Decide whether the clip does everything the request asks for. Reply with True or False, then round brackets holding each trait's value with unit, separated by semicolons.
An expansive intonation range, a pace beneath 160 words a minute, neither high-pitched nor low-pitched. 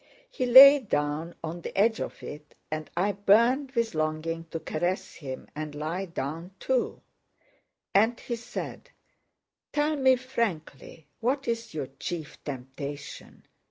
True (7.3 semitones; 135 wpm; 175 Hz)